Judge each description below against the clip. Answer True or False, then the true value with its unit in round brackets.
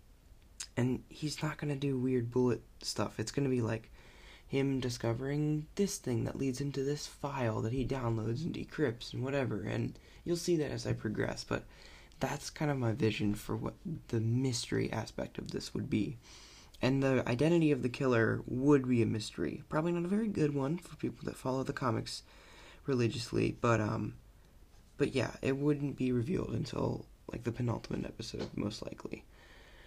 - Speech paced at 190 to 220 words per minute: False (180 wpm)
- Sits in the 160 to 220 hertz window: False (125 Hz)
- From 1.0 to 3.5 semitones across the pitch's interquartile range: False (4.0 semitones)